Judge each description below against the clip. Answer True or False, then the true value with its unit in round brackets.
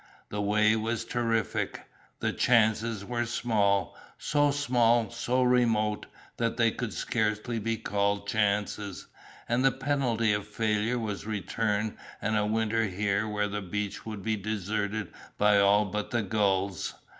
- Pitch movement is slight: True (2.0 semitones)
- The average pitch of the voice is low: True (110 Hz)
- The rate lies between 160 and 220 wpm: False (145 wpm)